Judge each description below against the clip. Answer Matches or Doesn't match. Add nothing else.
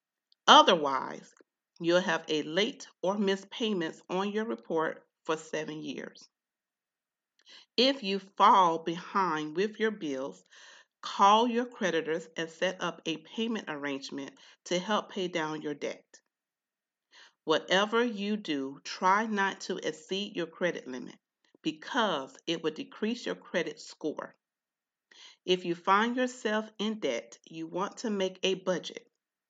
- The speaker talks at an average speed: Doesn't match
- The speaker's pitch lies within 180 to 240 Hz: Matches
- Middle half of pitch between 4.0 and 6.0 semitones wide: Matches